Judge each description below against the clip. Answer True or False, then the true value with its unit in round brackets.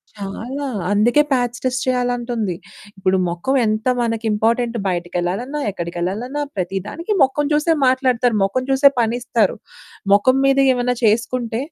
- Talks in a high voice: True (240 Hz)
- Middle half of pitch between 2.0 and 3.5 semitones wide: False (3.9 semitones)